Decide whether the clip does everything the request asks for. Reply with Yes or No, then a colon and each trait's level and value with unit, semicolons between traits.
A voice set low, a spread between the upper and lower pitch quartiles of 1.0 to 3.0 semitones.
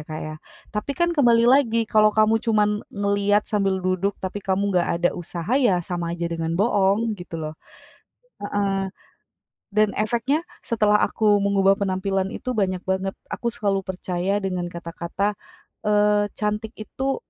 No: high, 200 Hz; narrow, 2.5 semitones